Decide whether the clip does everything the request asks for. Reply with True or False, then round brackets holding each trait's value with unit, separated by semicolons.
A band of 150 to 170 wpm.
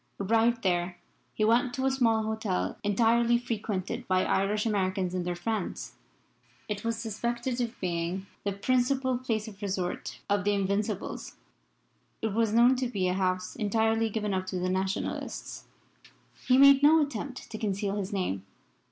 True (160 wpm)